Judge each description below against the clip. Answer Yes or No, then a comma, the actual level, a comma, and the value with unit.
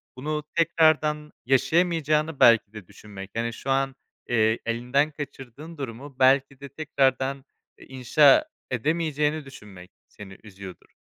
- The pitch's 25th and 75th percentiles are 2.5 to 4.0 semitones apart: No, average, 4.5 semitones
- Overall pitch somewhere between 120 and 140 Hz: Yes, low, 135 Hz